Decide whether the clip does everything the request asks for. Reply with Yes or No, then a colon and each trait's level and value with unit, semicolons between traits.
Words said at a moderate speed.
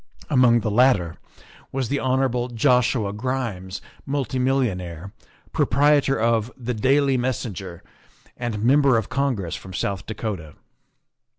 No: slow, 115 wpm